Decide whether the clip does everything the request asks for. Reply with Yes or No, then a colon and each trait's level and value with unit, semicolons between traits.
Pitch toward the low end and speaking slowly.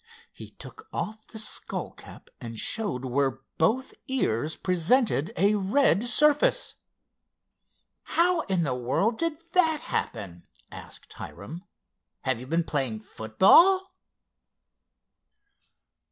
No: high, 190 Hz; slow, 110 wpm